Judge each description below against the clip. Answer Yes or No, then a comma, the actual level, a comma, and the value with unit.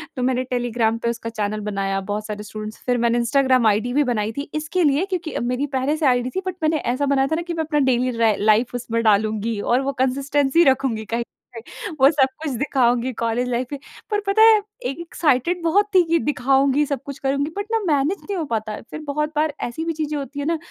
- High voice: Yes, very high, 270 Hz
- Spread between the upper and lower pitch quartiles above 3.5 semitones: Yes, average, 4.5 semitones